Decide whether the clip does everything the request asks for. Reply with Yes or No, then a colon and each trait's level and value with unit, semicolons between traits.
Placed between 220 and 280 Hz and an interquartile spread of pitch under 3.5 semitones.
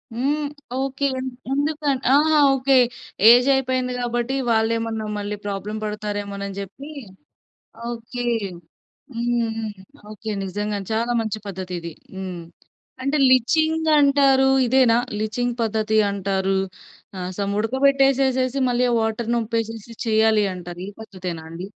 No: high, 230 Hz; average, 4.0 semitones